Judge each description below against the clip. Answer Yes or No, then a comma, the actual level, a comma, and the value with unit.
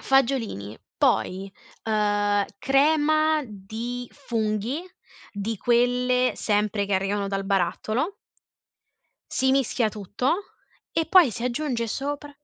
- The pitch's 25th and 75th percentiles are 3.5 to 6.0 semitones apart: Yes, average, 4.7 semitones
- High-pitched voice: Yes, high, 235 Hz